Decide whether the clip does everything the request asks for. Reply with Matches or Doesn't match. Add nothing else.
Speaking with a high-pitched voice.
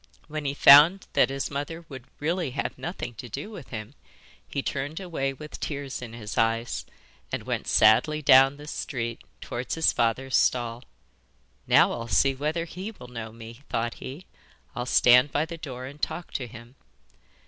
Doesn't match